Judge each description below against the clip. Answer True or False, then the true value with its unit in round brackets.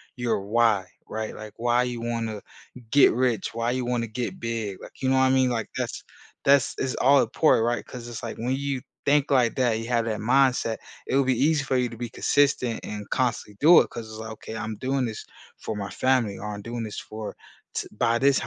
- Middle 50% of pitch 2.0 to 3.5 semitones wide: True (2.8 semitones)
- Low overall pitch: True (120 Hz)